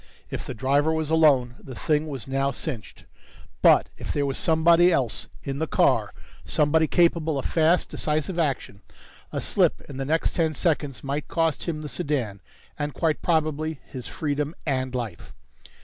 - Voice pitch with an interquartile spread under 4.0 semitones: Yes, average, 2.9 semitones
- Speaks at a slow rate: No, average, 165 wpm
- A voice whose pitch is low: No, medium, 150 Hz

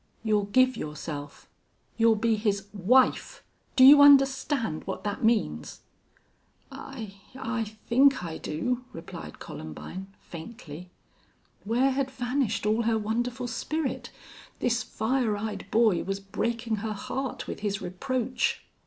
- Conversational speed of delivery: No, slow, 125 wpm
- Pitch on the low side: No, high, 225 Hz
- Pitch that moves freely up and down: No, average, 4.4 semitones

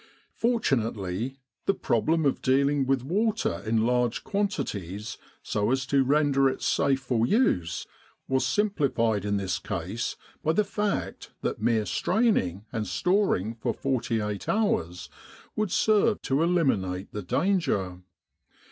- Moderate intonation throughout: No, wide, 8.2 semitones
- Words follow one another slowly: Yes, slow, 130 wpm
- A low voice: Yes, low, 130 Hz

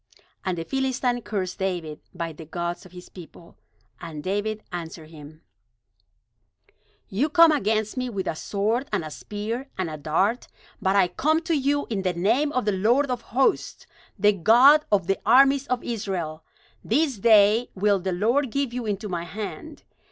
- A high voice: Yes, high, 210 Hz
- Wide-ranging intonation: Yes, wide, 5.9 semitones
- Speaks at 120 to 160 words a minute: No, average, 175 wpm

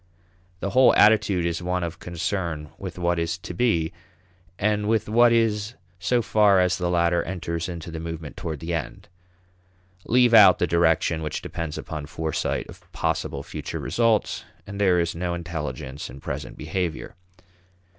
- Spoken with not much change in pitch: No, average, 3.8 semitones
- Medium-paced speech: Yes, average, 160 wpm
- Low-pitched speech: Yes, very low, 85 Hz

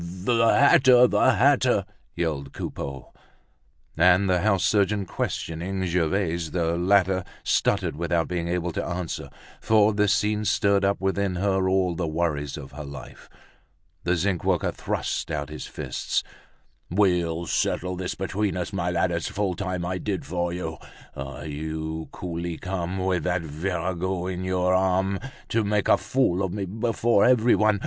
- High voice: No, very low, 90 Hz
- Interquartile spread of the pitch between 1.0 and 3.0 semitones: Yes, average, 2.7 semitones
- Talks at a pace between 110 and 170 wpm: Yes, average, 155 wpm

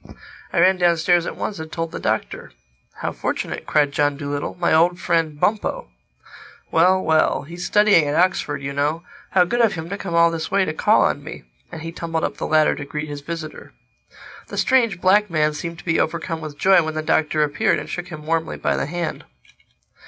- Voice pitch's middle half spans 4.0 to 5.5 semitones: No, narrow, 2.5 semitones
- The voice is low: No, medium, 165 Hz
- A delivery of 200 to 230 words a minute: Yes, fast, 205 wpm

